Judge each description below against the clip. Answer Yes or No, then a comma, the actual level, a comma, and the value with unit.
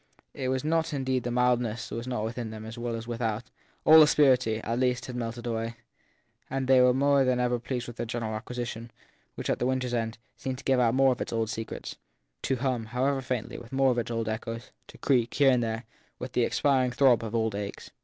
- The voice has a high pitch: No, low, 125 Hz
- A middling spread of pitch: No, narrow, 2.2 semitones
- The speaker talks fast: Yes, fast, 230 wpm